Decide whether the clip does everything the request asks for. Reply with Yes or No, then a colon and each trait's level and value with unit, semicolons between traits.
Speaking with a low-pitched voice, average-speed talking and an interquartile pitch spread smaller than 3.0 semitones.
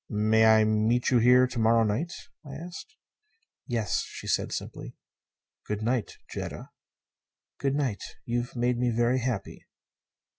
Yes: low, 120 Hz; average, 145 wpm; narrow, 2.5 semitones